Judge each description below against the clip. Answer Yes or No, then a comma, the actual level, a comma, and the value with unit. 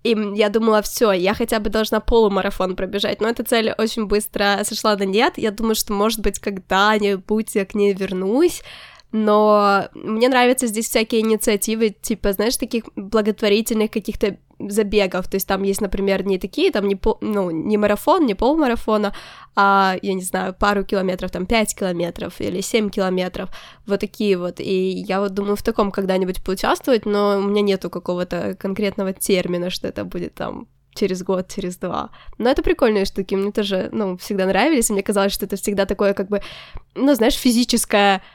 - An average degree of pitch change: No, narrow, 2.2 semitones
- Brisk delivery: Yes, fast, 180 wpm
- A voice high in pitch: Yes, high, 205 Hz